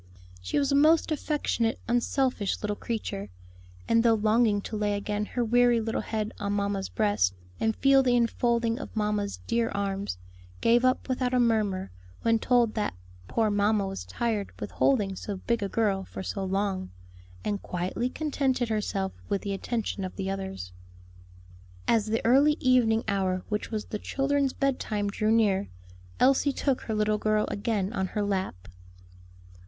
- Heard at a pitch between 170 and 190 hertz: No, high, 215 Hz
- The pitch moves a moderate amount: Yes, average, 3.1 semitones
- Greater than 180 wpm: No, average, 165 wpm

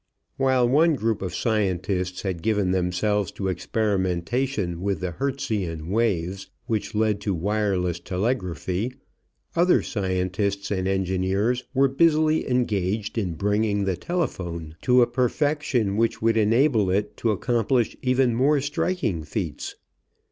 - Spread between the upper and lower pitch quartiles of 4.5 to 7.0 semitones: Yes, average, 5.0 semitones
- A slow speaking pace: Yes, slow, 125 wpm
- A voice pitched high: No, low, 105 Hz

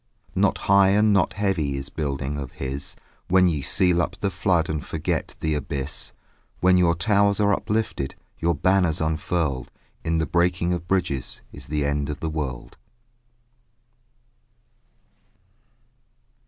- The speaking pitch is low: Yes, very low, 85 Hz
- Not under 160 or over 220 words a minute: No, average, 140 wpm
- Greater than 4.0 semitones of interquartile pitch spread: Yes, average, 4.4 semitones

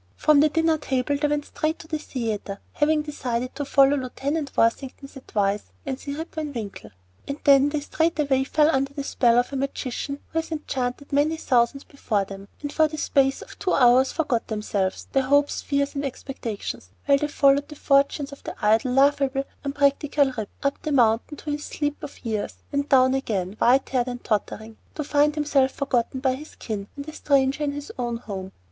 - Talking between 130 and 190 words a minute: No, average, 200 wpm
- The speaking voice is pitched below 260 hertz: No, very high, 275 Hz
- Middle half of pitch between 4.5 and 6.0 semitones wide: No, average, 3.0 semitones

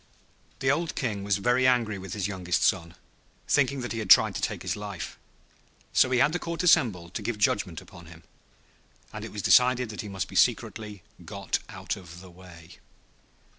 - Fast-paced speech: No, average, 195 wpm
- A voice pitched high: No, low, 105 Hz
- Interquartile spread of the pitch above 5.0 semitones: Yes, wide, 5.4 semitones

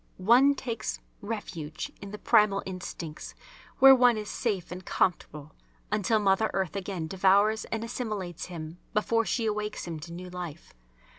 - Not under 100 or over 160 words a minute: Yes, average, 150 wpm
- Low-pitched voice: No, high, 195 Hz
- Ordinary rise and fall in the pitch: Yes, average, 3.7 semitones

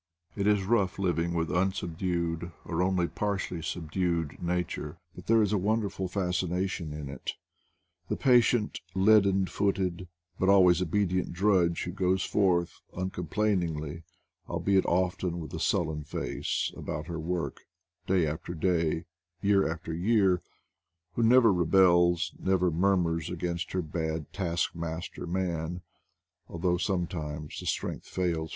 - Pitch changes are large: No, narrow, 2.4 semitones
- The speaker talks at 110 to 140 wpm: Yes, slow, 135 wpm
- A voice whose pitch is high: No, very low, 90 Hz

